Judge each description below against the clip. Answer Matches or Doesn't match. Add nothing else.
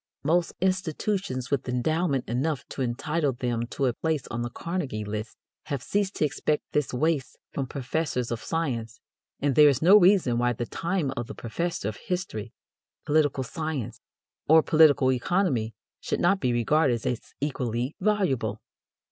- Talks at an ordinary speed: Matches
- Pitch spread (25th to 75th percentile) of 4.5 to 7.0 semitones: Matches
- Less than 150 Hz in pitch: Matches